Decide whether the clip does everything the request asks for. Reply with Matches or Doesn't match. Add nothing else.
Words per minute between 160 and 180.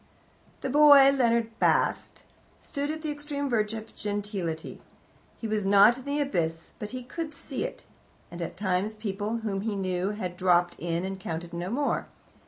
Matches